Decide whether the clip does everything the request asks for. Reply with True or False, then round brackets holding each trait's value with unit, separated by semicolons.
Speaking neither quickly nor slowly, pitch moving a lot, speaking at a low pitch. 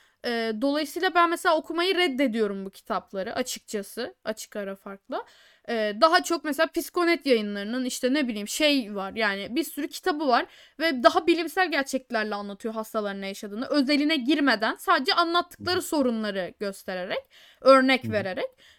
False (130 wpm; 7.2 semitones; 265 Hz)